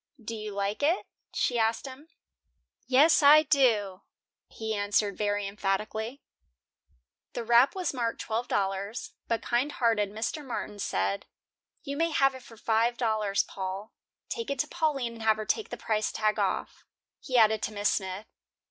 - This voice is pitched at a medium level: No, high, 225 Hz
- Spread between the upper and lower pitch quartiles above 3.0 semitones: Yes, average, 4.1 semitones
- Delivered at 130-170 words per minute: Yes, average, 165 wpm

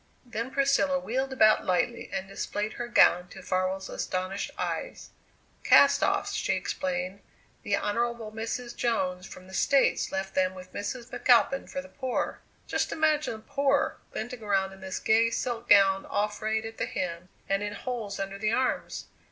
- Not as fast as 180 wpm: Yes, average, 170 wpm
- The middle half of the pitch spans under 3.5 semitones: No, average, 4.4 semitones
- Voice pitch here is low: No, high, 215 Hz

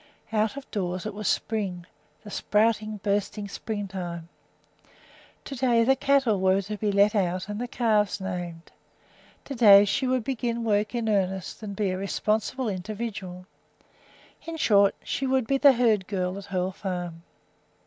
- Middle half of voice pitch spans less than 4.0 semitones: Yes, average, 3.4 semitones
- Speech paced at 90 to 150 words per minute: No, average, 160 wpm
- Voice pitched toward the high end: Yes, high, 210 Hz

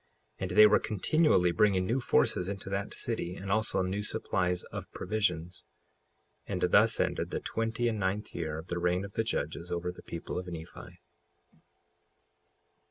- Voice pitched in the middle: No, very low, 95 Hz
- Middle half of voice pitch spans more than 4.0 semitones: No, average, 3.2 semitones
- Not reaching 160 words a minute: No, average, 170 wpm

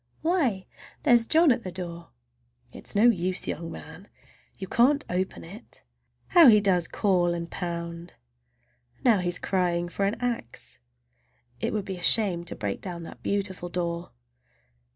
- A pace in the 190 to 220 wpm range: No, average, 155 wpm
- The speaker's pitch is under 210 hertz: Yes, medium, 185 Hz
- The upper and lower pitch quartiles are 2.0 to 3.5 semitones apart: No, average, 4.3 semitones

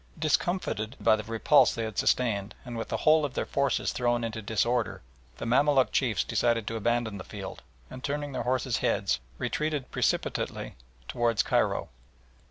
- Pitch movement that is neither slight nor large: Yes, average, 3.4 semitones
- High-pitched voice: No, low, 120 Hz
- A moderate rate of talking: Yes, average, 165 wpm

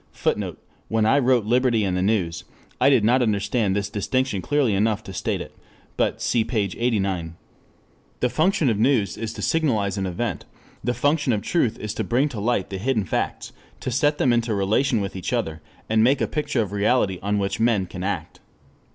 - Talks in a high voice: No, low, 110 Hz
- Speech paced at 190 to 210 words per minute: Yes, fast, 205 wpm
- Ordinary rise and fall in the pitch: Yes, average, 4.2 semitones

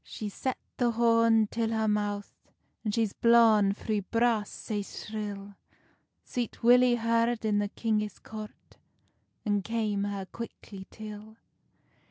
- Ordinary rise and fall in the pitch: No, narrow, 2.0 semitones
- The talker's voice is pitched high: Yes, high, 220 Hz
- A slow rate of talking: Yes, slow, 130 wpm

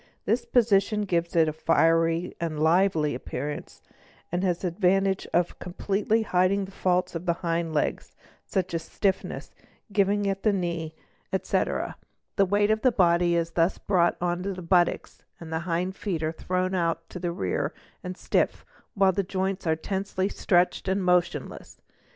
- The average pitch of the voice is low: No, medium, 180 Hz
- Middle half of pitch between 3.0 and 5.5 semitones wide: No, narrow, 2.6 semitones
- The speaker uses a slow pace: No, average, 165 wpm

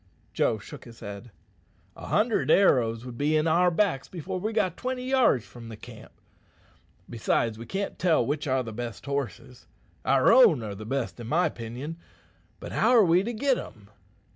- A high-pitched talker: No, medium, 140 Hz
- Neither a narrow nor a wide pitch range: No, wide, 8.3 semitones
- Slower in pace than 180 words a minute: No, average, 185 wpm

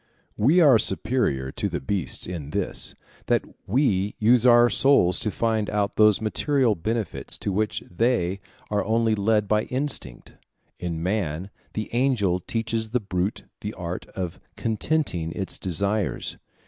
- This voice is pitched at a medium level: No, low, 105 Hz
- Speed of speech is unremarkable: Yes, average, 145 wpm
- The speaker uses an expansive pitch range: No, average, 3.9 semitones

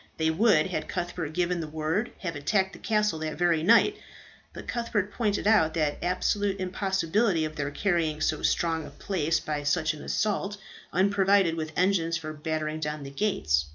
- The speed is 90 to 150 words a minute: No, average, 175 wpm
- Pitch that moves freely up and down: No, average, 4.2 semitones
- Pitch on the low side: No, medium, 170 Hz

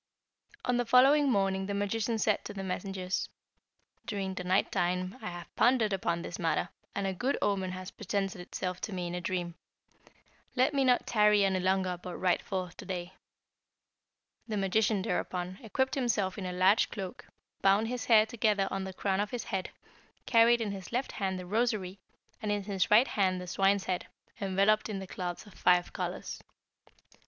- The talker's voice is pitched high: Yes, high, 195 Hz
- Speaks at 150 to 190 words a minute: Yes, average, 185 wpm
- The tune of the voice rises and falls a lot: No, average, 2.7 semitones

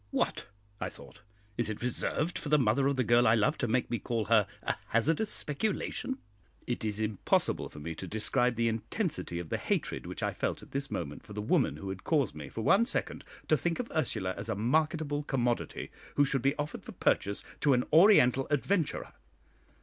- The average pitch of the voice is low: Yes, low, 125 Hz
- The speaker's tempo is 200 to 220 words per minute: Yes, fast, 205 wpm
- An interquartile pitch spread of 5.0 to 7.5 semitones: Yes, wide, 5.5 semitones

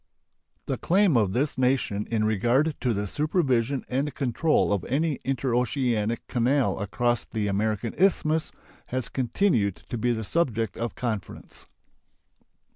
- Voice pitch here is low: Yes, low, 120 Hz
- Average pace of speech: No, slow, 130 wpm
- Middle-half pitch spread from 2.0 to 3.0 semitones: No, average, 4.3 semitones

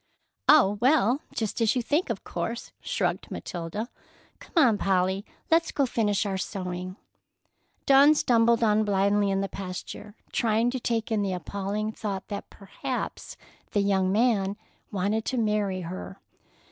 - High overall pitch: Yes, high, 210 Hz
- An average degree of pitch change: Yes, average, 3.3 semitones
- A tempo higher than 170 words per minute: No, average, 145 wpm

